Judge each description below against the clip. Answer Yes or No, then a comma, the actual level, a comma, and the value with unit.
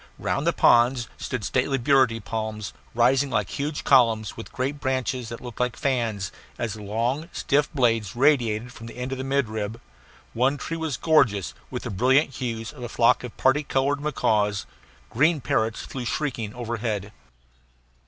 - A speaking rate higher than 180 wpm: No, average, 165 wpm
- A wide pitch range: No, average, 3.3 semitones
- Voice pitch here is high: No, low, 125 Hz